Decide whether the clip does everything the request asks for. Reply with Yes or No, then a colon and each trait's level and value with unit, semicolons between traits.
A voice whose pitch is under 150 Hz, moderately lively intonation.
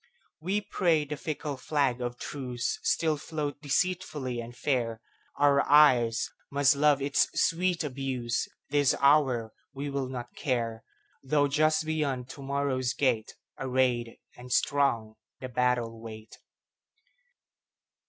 Yes: low, 135 Hz; average, 3.3 semitones